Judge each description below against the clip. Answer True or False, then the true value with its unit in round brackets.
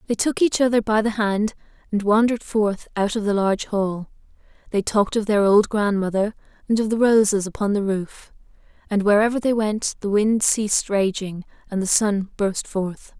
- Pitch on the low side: False (210 Hz)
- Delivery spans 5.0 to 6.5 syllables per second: True (5.1 syllables/s)